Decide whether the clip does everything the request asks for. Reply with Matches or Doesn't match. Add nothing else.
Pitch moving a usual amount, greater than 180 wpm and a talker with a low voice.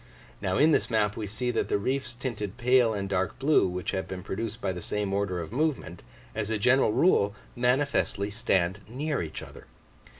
Matches